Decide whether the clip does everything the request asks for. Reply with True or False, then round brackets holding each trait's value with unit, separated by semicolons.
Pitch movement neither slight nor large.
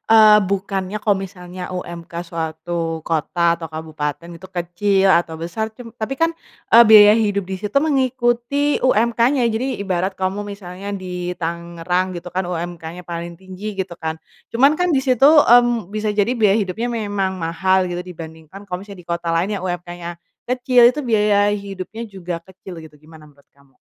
True (4.1 semitones)